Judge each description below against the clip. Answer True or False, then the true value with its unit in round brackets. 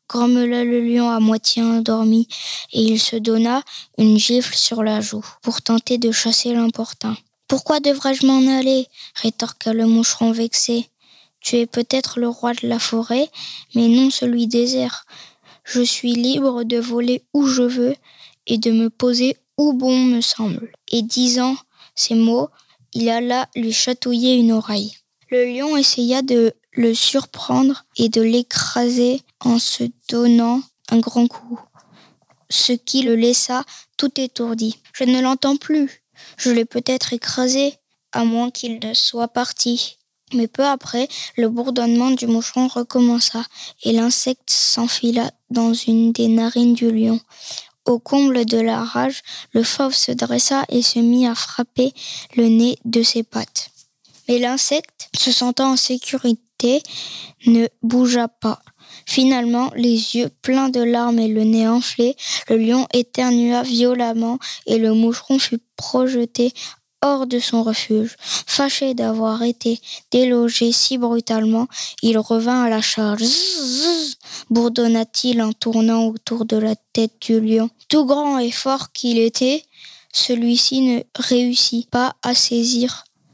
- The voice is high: True (240 Hz)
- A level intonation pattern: True (1.8 semitones)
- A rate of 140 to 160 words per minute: True (150 wpm)